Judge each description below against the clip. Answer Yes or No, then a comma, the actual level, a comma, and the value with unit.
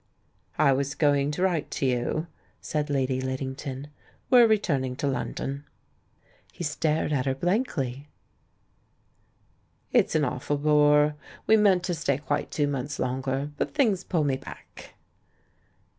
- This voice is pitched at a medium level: Yes, medium, 145 Hz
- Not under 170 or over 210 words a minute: No, average, 140 wpm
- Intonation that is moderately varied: Yes, average, 3.1 semitones